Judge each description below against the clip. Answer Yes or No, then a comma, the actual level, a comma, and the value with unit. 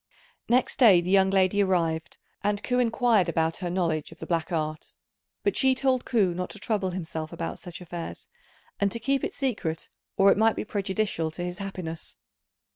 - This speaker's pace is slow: No, average, 190 wpm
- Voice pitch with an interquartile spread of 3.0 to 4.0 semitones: No, average, 4.5 semitones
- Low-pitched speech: No, high, 190 Hz